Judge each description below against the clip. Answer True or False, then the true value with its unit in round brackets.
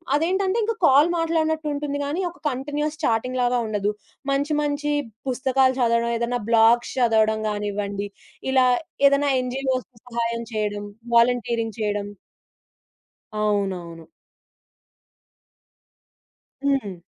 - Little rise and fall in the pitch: False (4.8 semitones)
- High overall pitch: True (245 Hz)